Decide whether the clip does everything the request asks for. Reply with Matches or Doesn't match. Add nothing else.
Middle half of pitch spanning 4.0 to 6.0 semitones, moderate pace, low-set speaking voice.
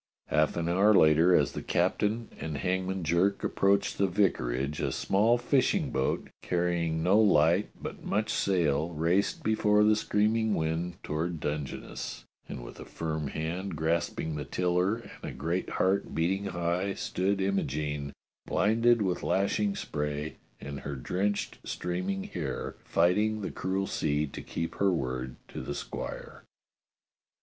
Matches